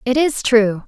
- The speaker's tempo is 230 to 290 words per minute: No, fast, 205 wpm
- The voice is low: No, high, 240 Hz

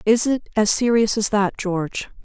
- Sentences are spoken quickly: No, average, 190 wpm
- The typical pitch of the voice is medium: No, high, 215 Hz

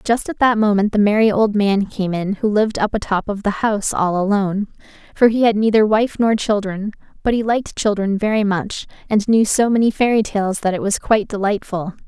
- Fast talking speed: Yes, fast, 215 wpm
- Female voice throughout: Yes, female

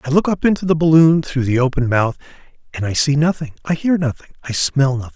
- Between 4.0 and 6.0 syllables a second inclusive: No, 6.2 syllables/s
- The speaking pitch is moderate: Yes, medium, 145 Hz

